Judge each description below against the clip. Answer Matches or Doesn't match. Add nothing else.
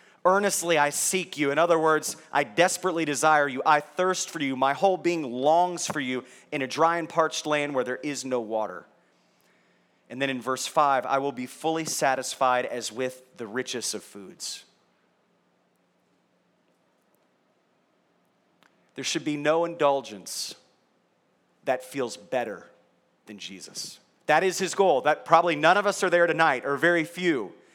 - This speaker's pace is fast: Doesn't match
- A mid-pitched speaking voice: Matches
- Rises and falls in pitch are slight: Doesn't match